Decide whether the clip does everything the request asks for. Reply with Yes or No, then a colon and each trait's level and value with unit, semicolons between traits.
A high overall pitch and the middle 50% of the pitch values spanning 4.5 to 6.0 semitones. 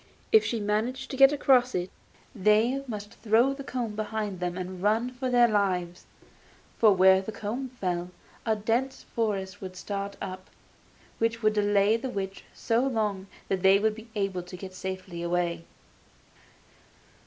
No: high, 210 Hz; average, 3.6 semitones